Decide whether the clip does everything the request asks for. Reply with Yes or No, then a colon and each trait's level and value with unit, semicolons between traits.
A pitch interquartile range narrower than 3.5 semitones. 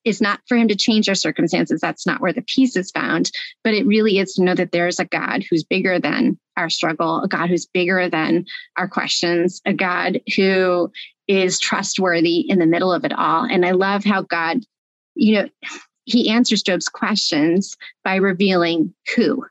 No: average, 3.8 semitones